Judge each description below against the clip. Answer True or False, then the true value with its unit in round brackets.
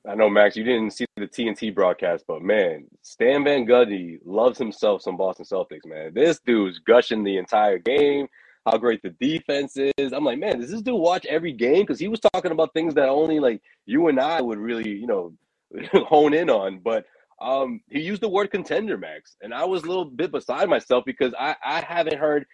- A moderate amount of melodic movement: False (8.4 semitones)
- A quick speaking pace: True (215 wpm)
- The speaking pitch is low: False (145 Hz)